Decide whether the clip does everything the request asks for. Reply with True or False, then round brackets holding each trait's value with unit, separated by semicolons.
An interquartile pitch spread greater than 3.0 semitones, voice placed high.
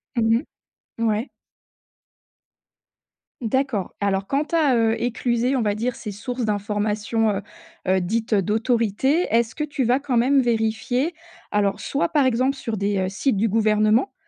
True (3.7 semitones; 230 Hz)